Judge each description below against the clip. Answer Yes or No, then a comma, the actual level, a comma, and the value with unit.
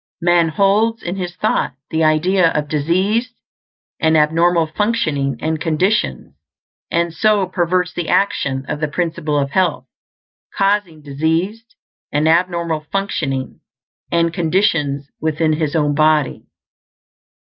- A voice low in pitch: No, medium, 165 Hz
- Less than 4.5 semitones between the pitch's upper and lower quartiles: Yes, average, 3.4 semitones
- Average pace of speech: No, slow, 120 wpm